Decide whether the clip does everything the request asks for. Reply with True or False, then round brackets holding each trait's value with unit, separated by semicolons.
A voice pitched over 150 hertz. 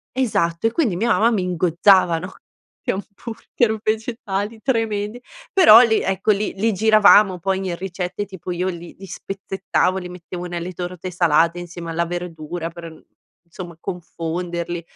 True (185 Hz)